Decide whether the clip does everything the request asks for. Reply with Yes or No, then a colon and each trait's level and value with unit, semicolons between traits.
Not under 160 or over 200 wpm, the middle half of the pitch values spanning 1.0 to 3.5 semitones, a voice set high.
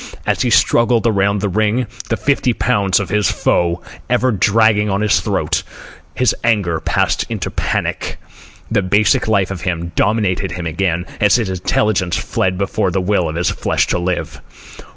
No: average, 170 wpm; average, 3.2 semitones; low, 100 Hz